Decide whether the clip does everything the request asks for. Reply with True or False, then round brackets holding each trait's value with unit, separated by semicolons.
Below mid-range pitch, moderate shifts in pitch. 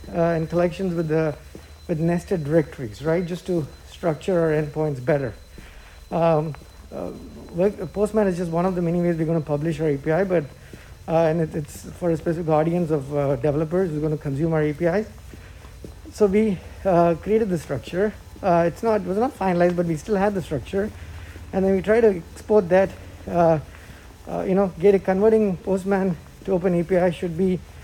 False (170 Hz; 3.7 semitones)